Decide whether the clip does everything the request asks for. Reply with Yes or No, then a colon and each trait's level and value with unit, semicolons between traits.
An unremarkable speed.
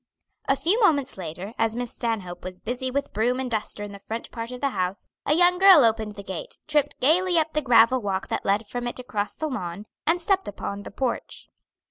No: fast, 220 wpm